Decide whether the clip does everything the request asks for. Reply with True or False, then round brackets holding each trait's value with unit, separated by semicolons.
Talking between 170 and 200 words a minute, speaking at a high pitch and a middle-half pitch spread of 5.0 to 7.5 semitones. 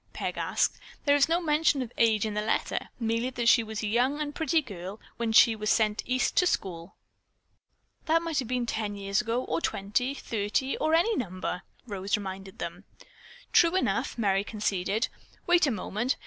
True (185 wpm; 230 Hz; 5.4 semitones)